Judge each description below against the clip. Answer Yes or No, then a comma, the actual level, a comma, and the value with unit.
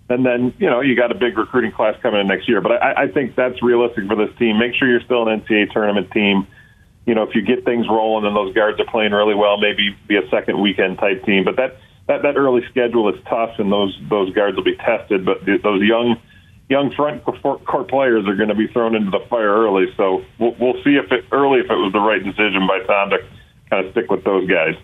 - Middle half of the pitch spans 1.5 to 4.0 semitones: Yes, average, 2.8 semitones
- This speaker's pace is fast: Yes, fast, 255 wpm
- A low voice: Yes, low, 110 Hz